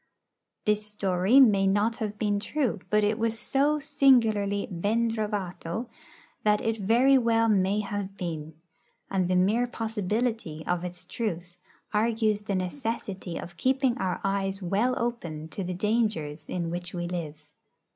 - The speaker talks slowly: No, average, 145 wpm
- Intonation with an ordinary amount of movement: Yes, average, 3.9 semitones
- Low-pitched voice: No, high, 205 Hz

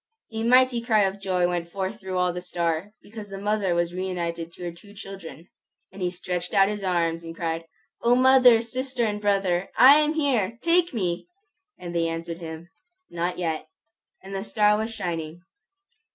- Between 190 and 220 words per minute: No, average, 180 wpm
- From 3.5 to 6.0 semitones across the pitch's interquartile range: Yes, average, 4.2 semitones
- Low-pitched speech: No, high, 190 Hz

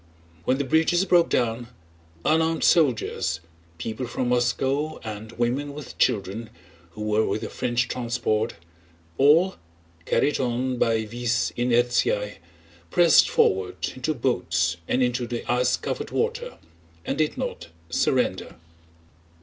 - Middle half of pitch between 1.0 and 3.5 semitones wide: No, average, 4.4 semitones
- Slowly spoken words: Yes, slow, 115 wpm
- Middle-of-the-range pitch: No, low, 120 Hz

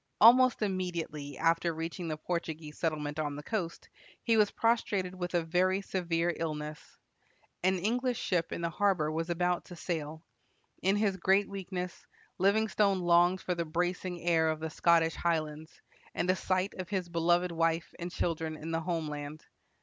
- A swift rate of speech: No, average, 165 wpm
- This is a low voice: No, medium, 175 Hz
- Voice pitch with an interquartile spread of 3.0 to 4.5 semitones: No, narrow, 2.5 semitones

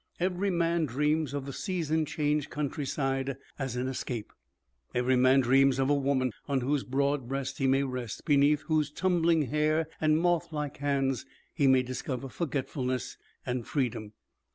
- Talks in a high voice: No, medium, 140 Hz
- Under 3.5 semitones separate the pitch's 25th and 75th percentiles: Yes, average, 2.8 semitones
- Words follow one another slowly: No, average, 155 wpm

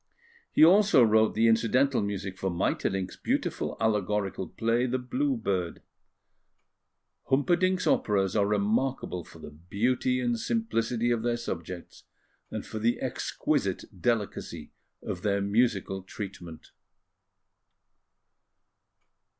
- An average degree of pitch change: Yes, average, 4.4 semitones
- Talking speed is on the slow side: Yes, slow, 110 wpm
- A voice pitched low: Yes, low, 110 Hz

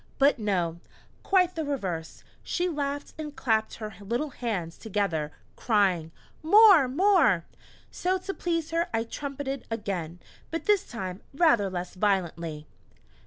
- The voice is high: Yes, high, 230 Hz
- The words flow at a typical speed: No, slow, 130 wpm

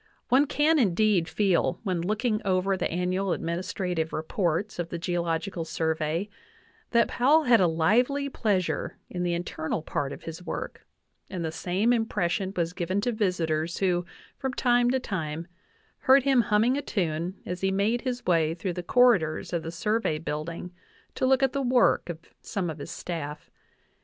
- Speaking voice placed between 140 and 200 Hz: Yes, medium, 185 Hz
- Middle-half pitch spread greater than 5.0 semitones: Yes, wide, 5.6 semitones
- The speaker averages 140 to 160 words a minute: No, average, 175 wpm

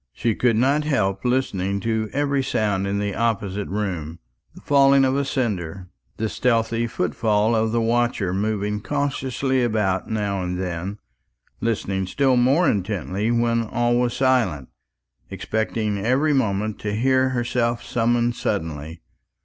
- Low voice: Yes, low, 110 Hz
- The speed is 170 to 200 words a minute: No, average, 140 wpm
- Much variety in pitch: No, average, 3.9 semitones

